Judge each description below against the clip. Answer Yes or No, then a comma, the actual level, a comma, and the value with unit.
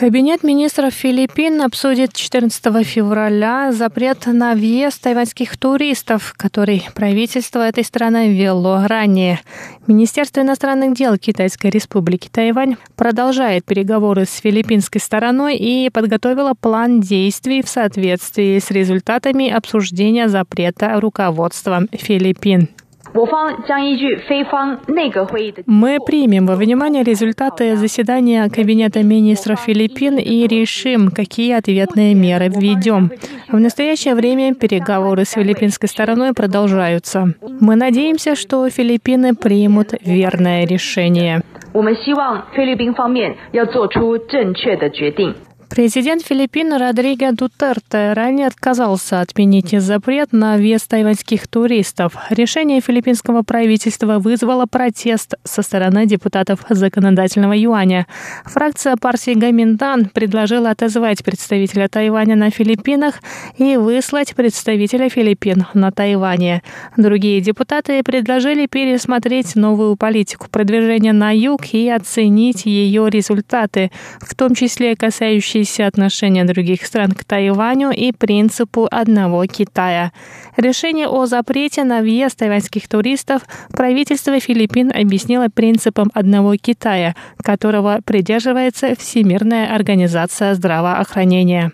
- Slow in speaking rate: Yes, slow, 100 wpm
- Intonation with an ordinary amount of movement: Yes, average, 3.7 semitones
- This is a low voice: No, high, 225 Hz